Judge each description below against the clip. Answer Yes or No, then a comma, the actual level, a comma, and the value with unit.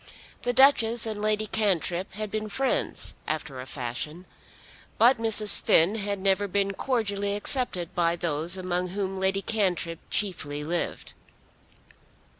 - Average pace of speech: No, slow, 130 wpm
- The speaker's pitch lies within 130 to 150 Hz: No, high, 195 Hz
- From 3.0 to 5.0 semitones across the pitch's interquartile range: Yes, average, 3.7 semitones